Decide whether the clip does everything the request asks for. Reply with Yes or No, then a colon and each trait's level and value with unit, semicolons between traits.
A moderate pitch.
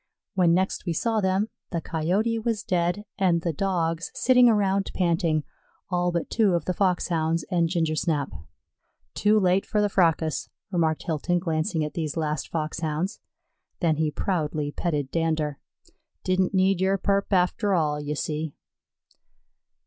Yes: medium, 175 Hz